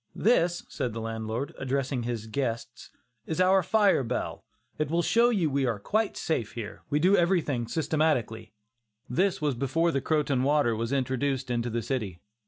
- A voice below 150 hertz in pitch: Yes, low, 135 Hz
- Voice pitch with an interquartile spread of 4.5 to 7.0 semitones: Yes, wide, 5.6 semitones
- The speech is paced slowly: No, average, 170 wpm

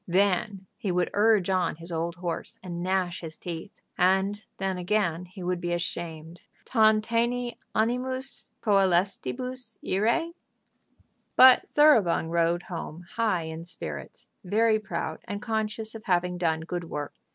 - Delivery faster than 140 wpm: No, slow, 135 wpm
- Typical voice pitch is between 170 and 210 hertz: Yes, medium, 185 Hz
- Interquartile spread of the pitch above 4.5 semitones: No, average, 4.1 semitones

